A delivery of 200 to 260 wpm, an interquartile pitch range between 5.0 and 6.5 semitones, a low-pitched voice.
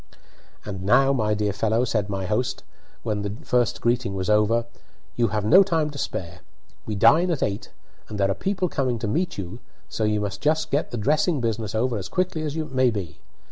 Yes: fast, 205 wpm; wide, 5.5 semitones; low, 115 Hz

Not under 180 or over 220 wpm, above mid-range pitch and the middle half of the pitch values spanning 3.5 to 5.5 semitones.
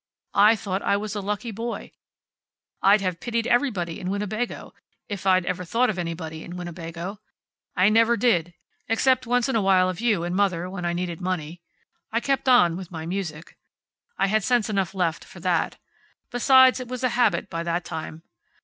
Yes: average, 185 wpm; high, 195 Hz; average, 4.8 semitones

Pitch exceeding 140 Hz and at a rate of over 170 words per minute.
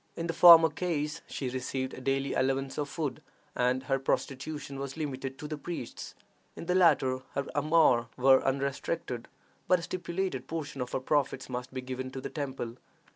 No: low, 135 Hz; average, 180 wpm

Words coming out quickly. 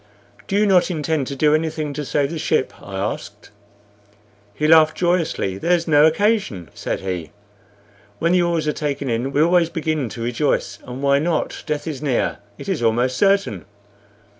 No: average, 175 wpm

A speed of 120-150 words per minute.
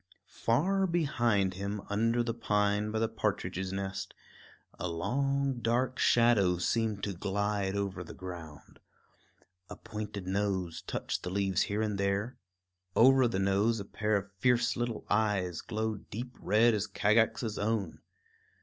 Yes: average, 140 wpm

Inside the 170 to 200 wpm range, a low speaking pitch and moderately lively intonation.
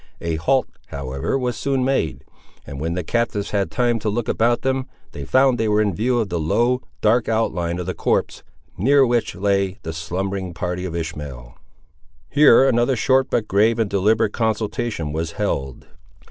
No: average, 175 wpm; low, 105 Hz; wide, 5.9 semitones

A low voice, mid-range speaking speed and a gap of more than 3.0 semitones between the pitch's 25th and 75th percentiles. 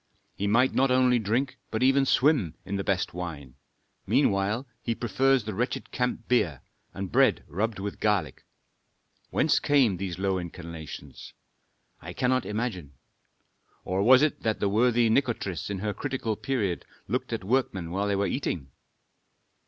Yes: low, 105 Hz; average, 150 wpm; average, 5.0 semitones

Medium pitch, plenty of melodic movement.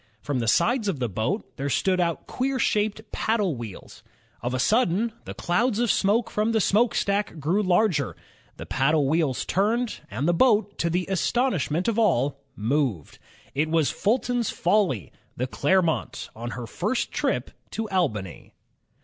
Yes: medium, 180 Hz; wide, 7.7 semitones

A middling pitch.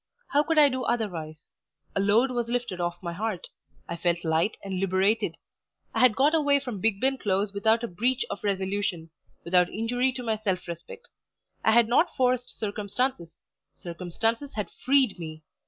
No: high, 210 Hz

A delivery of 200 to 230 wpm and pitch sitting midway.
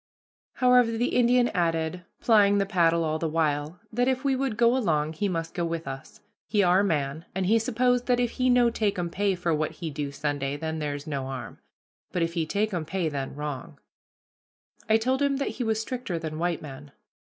Yes: fast, 205 wpm; medium, 175 Hz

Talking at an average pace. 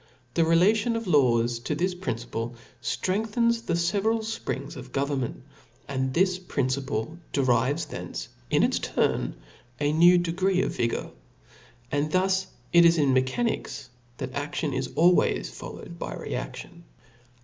Yes: average, 145 wpm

